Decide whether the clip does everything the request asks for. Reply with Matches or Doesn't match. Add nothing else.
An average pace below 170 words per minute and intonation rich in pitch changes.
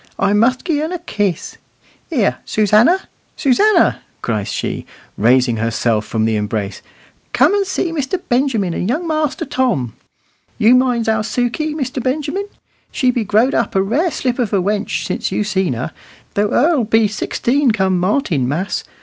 Matches